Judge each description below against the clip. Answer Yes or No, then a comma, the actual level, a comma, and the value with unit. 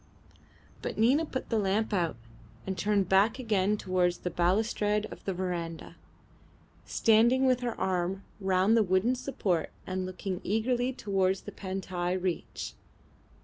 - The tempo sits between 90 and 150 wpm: Yes, average, 140 wpm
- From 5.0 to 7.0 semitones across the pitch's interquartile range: No, average, 3.3 semitones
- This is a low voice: No, high, 195 Hz